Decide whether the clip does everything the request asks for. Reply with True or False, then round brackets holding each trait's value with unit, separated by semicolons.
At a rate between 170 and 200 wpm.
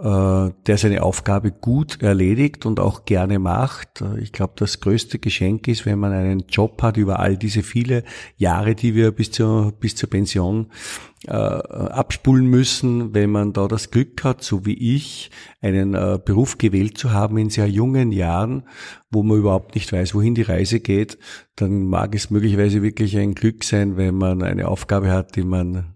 True (180 wpm)